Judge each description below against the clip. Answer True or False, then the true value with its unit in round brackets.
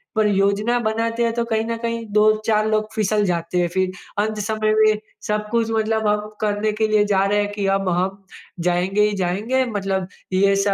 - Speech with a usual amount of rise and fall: False (1.9 semitones)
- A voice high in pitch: True (210 Hz)